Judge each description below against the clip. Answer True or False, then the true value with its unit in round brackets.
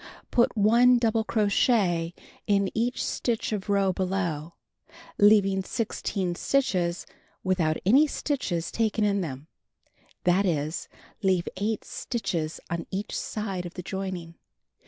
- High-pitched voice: True (195 Hz)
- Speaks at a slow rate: True (120 wpm)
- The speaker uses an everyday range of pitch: True (3.9 semitones)